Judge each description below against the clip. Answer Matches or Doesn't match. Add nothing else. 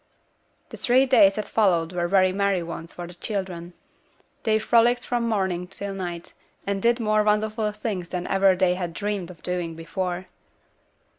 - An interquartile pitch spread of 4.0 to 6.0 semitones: Doesn't match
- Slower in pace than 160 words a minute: Doesn't match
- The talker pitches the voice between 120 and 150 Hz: Doesn't match